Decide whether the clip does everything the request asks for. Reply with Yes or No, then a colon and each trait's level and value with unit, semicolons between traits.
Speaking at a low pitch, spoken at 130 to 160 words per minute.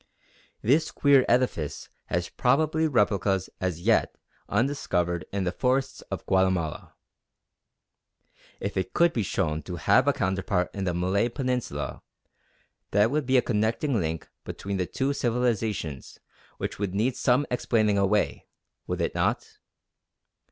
Yes: low, 105 Hz; slow, 135 wpm